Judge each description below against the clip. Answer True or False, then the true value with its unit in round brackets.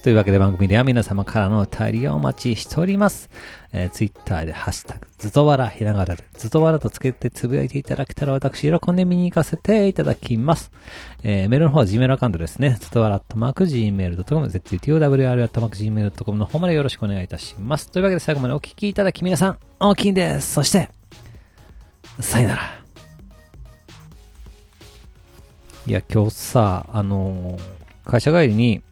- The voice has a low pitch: True (115 Hz)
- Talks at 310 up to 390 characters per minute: False (425 characters per minute)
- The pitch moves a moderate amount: False (7.5 semitones)